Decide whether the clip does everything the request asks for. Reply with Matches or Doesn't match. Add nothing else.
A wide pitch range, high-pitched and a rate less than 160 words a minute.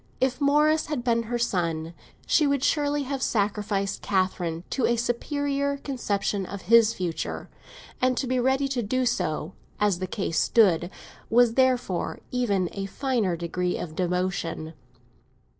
Matches